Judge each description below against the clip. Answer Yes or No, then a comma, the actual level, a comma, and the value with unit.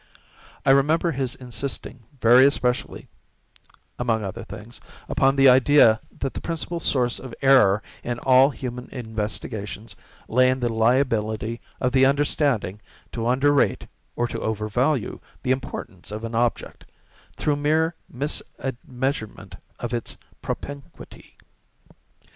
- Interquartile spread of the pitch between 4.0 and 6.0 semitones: No, average, 3.3 semitones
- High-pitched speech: No, low, 125 Hz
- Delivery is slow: Yes, slow, 125 wpm